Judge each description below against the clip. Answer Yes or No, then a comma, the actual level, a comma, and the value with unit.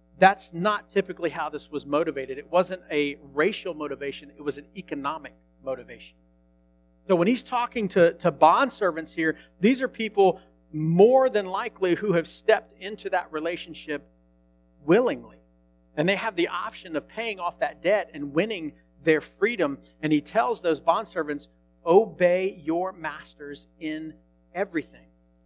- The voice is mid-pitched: Yes, medium, 160 Hz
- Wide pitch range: Yes, wide, 6.1 semitones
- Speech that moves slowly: No, average, 150 wpm